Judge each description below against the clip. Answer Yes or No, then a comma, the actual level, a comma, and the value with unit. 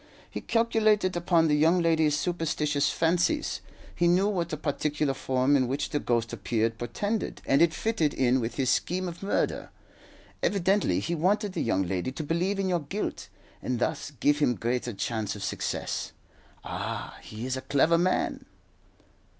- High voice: No, medium, 155 Hz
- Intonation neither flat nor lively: No, wide, 5.9 semitones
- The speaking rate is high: No, average, 165 wpm